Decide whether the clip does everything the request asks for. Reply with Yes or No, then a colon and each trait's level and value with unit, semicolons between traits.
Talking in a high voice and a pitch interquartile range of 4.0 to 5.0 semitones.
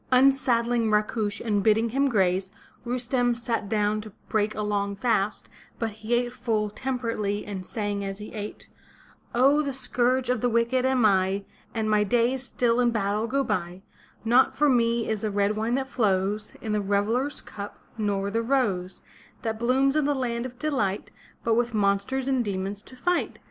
No: high, 225 Hz; average, 3.3 semitones